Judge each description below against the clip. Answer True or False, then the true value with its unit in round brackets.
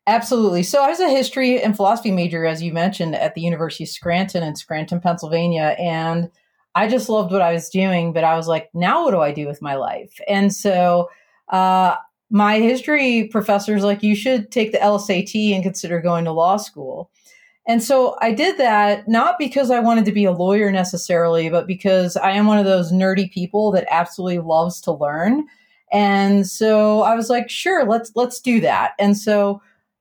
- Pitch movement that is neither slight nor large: True (4.5 semitones)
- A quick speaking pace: False (195 wpm)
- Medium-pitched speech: False (195 Hz)